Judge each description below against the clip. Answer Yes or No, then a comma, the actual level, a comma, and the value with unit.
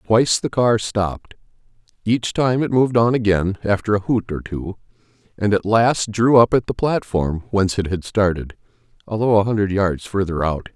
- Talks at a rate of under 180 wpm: No, average, 185 wpm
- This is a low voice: Yes, low, 105 Hz